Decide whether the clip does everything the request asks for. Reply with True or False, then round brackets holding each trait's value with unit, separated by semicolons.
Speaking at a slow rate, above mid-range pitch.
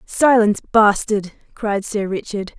True (115 wpm; 210 Hz)